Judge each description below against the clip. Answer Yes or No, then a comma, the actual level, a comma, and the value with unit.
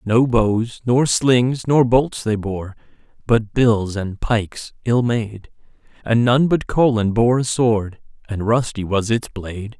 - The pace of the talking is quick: No, average, 160 wpm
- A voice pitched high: No, low, 115 Hz